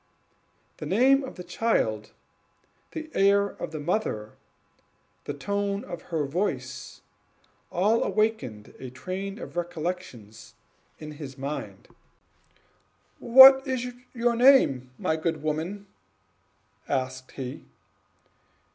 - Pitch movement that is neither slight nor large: No, wide, 7.9 semitones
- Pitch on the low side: No, medium, 175 Hz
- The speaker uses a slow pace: Yes, slow, 105 wpm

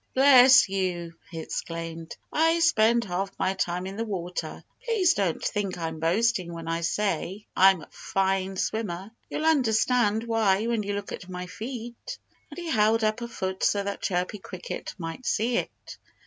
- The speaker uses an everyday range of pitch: Yes, average, 4.4 semitones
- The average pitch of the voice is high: Yes, high, 200 Hz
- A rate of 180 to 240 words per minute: No, average, 170 wpm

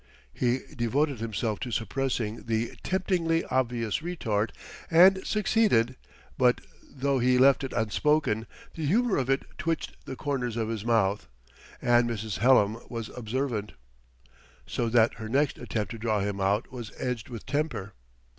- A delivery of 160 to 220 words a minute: No, average, 145 wpm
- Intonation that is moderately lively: Yes, average, 4.0 semitones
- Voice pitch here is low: Yes, low, 120 Hz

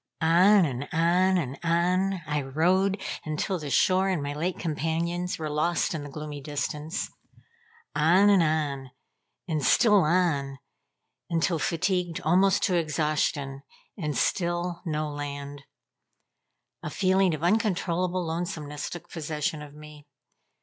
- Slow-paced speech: Yes, slow, 130 wpm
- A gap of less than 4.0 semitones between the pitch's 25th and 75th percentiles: Yes, average, 3.4 semitones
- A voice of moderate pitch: Yes, medium, 165 Hz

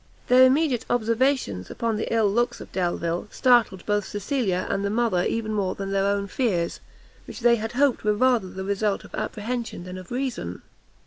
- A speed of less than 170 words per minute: No, average, 185 wpm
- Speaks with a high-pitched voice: Yes, high, 215 Hz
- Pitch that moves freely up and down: No, average, 4.0 semitones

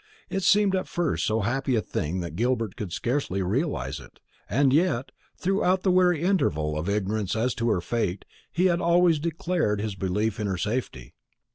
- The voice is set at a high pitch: No, low, 115 Hz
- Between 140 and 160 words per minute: No, average, 180 wpm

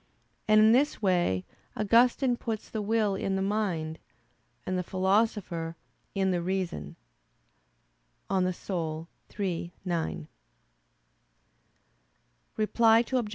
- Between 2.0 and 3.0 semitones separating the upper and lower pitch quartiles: No, average, 4.0 semitones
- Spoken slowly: Yes, slow, 105 wpm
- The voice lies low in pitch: No, high, 195 Hz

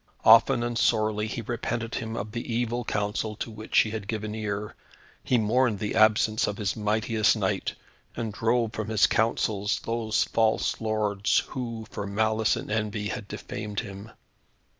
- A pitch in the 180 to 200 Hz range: No, low, 110 Hz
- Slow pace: No, average, 160 wpm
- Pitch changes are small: Yes, narrow, 1.5 semitones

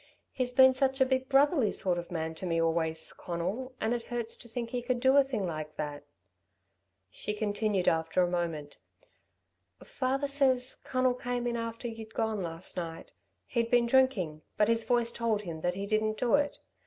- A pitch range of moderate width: No, wide, 6.5 semitones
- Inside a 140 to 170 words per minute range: No, average, 190 wpm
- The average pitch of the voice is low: No, high, 225 Hz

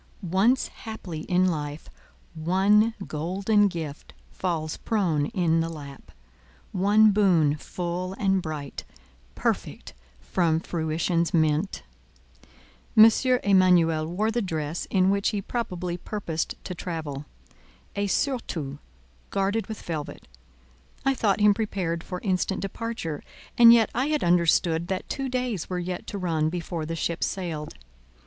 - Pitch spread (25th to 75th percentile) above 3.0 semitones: Yes, average, 4.1 semitones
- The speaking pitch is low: No, medium, 180 Hz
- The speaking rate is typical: No, slow, 125 wpm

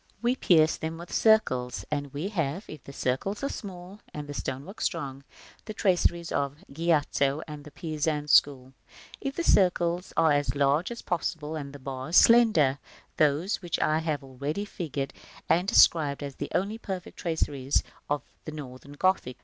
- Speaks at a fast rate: No, average, 165 wpm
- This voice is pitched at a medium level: Yes, medium, 155 Hz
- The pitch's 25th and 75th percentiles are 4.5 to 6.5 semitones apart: No, average, 4.1 semitones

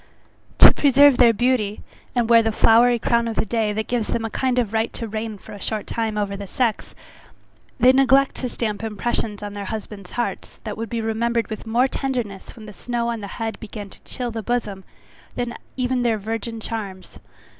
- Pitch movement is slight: Yes, narrow, 2.3 semitones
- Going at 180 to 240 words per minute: Yes, fast, 205 wpm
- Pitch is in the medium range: No, high, 225 Hz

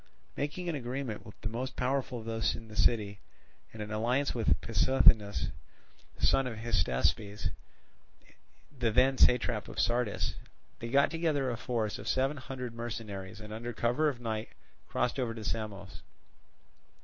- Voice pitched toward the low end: Yes, low, 115 Hz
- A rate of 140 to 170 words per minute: Yes, average, 150 wpm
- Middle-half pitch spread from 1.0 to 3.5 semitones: Yes, average, 3.2 semitones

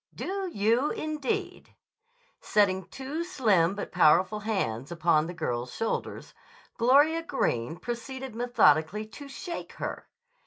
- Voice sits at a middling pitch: No, high, 215 Hz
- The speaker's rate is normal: No, slow, 115 wpm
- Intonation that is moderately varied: No, wide, 8.0 semitones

